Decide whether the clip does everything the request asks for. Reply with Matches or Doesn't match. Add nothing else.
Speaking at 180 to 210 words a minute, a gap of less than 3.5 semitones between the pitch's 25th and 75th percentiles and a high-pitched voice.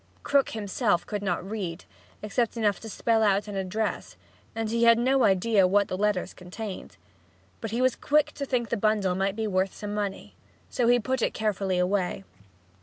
Matches